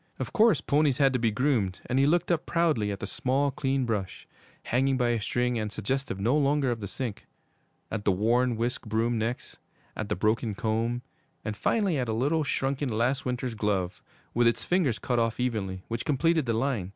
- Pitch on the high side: No, low, 120 Hz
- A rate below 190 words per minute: No, average, 200 wpm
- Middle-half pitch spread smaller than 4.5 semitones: Yes, average, 3.8 semitones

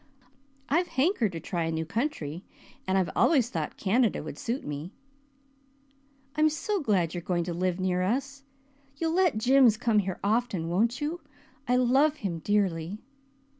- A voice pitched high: Yes, high, 215 Hz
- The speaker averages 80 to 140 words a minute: No, average, 165 wpm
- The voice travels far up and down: Yes, wide, 7.4 semitones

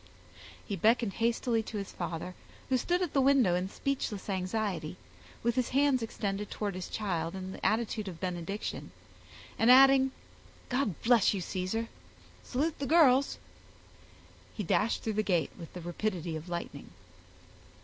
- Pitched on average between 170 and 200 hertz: No, high, 215 Hz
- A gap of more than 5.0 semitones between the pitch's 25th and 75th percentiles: Yes, wide, 5.4 semitones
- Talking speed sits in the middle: Yes, average, 150 wpm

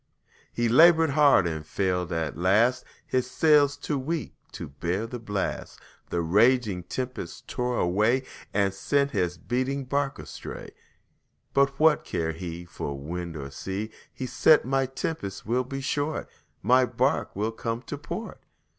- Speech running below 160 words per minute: Yes, average, 150 wpm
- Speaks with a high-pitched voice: No, low, 120 Hz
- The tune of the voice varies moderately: No, wide, 7.3 semitones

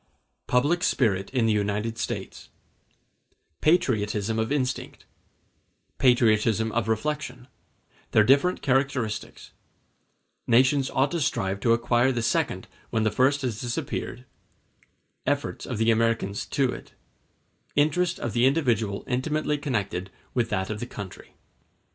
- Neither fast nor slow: No, slow, 110 wpm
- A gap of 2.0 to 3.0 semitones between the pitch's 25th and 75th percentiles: No, average, 4.0 semitones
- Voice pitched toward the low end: Yes, low, 120 Hz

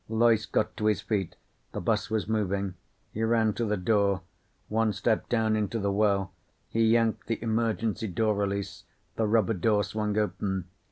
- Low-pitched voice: Yes, low, 110 Hz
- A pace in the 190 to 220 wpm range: No, average, 170 wpm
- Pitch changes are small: Yes, narrow, 1.9 semitones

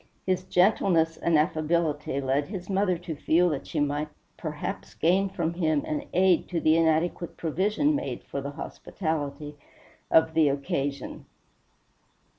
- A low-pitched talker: No, medium, 160 Hz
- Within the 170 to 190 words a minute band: No, average, 140 wpm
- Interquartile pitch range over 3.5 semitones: No, average, 3.2 semitones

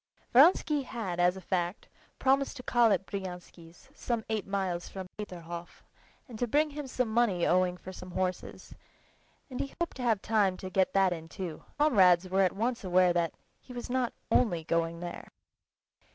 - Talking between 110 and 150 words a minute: No, average, 185 wpm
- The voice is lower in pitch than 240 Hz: Yes, high, 190 Hz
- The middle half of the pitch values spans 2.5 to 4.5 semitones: No, average, 5.3 semitones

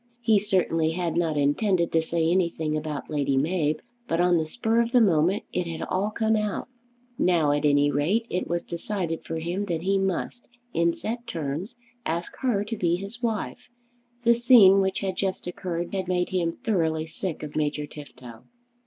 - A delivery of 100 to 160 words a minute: No, average, 185 wpm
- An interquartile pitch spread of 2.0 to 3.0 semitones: No, average, 4.0 semitones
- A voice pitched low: No, medium, 175 Hz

